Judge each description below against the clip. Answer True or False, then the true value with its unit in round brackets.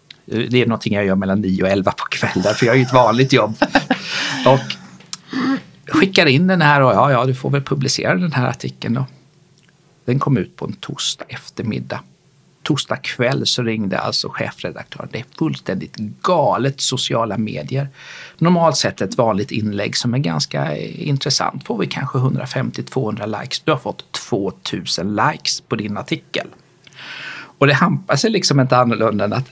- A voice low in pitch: True (130 Hz)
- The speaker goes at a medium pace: True (170 wpm)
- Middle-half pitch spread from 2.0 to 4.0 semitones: False (4.5 semitones)